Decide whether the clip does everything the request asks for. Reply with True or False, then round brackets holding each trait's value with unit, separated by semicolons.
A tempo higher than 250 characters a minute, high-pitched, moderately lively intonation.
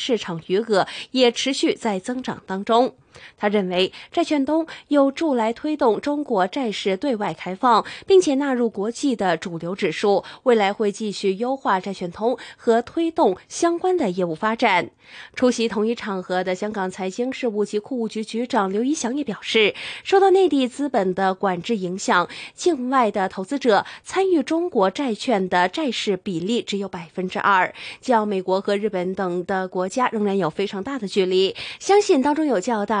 False (265 characters per minute; 225 Hz; 5.9 semitones)